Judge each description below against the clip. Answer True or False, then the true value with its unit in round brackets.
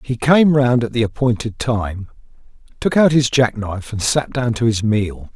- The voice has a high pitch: False (120 Hz)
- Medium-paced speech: True (190 wpm)